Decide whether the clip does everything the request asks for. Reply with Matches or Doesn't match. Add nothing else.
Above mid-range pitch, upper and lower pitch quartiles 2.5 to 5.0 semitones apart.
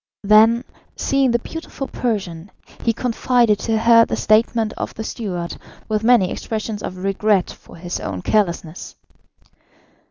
Matches